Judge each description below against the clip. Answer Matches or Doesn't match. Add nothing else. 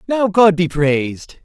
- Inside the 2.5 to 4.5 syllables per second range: Matches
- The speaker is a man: Matches